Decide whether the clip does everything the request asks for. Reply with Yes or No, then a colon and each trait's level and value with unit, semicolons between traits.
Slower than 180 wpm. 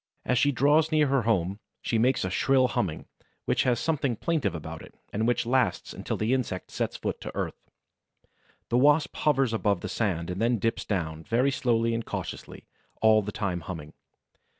No: average, 185 wpm